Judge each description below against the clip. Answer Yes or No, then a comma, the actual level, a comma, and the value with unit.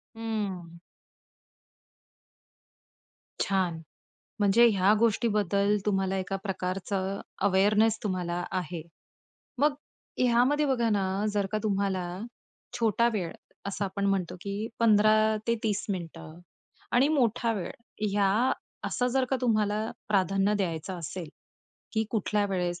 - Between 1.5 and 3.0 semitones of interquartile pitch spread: Yes, average, 2.7 semitones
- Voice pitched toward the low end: No, high, 200 Hz